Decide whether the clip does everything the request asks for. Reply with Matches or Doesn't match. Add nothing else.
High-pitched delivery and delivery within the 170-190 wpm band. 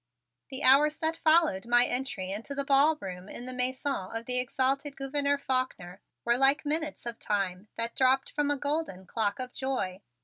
Matches